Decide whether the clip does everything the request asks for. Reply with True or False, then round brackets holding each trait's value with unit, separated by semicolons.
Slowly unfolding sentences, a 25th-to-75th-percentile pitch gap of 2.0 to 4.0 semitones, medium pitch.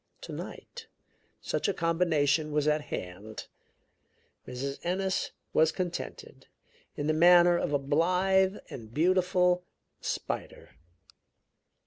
True (100 wpm; 3.7 semitones; 165 Hz)